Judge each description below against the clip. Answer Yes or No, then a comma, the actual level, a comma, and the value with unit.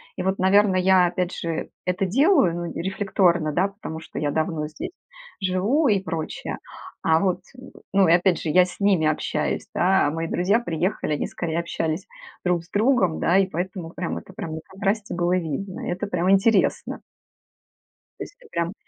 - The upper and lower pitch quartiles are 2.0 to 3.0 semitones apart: Yes, average, 2.7 semitones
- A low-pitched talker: No, medium, 180 Hz